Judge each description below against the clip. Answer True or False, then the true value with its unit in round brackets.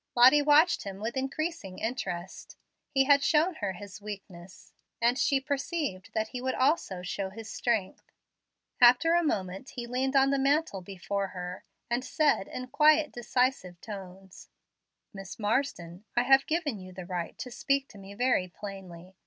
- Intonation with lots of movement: True (6.2 semitones)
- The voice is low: False (235 Hz)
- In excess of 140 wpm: True (160 wpm)